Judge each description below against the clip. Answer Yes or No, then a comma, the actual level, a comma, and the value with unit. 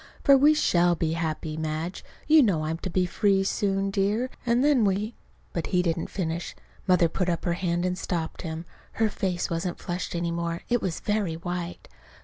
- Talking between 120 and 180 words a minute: No, average, 200 wpm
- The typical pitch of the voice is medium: Yes, medium, 180 Hz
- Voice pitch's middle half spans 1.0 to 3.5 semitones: Yes, average, 2.9 semitones